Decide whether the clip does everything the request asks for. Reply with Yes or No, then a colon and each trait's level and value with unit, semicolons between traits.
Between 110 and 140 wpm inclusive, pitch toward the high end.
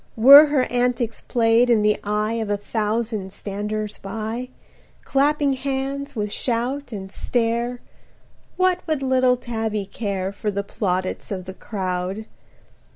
Yes: slow, 135 wpm; high, 225 Hz